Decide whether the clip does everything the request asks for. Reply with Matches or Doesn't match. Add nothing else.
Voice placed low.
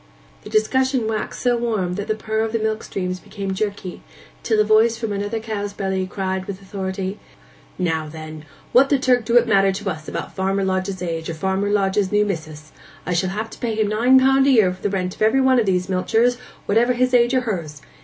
Doesn't match